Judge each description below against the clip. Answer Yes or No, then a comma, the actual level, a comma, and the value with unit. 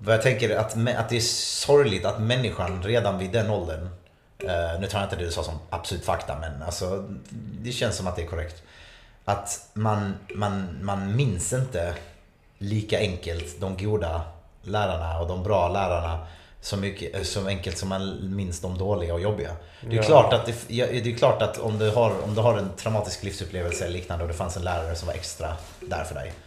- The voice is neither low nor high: No, very low, 95 Hz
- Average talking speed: No, fast, 205 wpm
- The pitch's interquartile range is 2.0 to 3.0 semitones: No, average, 3.6 semitones